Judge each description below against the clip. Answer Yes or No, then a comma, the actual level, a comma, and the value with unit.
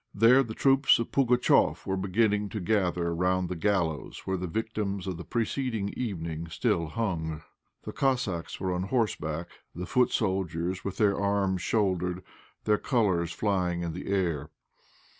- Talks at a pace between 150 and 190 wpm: Yes, average, 155 wpm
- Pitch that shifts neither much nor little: Yes, average, 4.0 semitones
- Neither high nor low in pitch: No, very low, 95 Hz